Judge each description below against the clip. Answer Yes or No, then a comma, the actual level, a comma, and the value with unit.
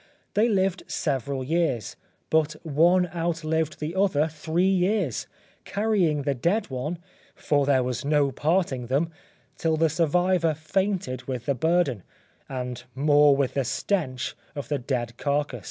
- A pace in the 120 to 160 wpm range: Yes, average, 140 wpm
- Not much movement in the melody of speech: No, average, 4.3 semitones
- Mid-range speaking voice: Yes, medium, 155 Hz